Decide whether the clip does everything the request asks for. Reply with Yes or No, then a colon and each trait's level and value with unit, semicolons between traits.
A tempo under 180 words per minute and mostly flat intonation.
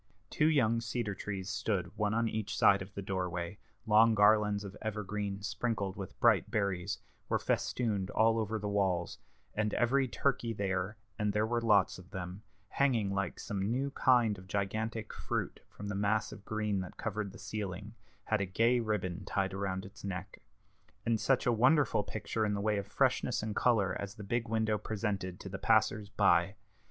No: average, 185 wpm; narrow, 2.2 semitones